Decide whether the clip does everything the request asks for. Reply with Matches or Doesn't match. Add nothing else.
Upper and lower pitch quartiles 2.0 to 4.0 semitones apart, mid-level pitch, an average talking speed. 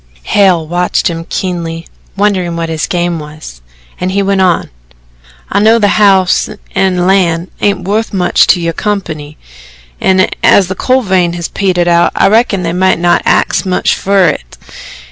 Matches